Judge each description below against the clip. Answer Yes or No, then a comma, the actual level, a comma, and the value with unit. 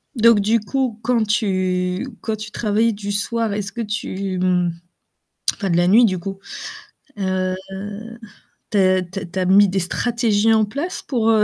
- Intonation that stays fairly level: No, average, 3.1 semitones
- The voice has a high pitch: Yes, high, 205 Hz